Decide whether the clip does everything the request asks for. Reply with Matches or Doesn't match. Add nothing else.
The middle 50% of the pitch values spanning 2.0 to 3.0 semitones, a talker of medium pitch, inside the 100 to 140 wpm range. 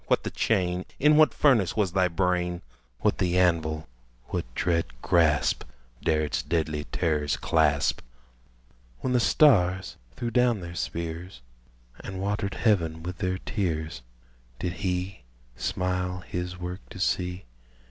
Doesn't match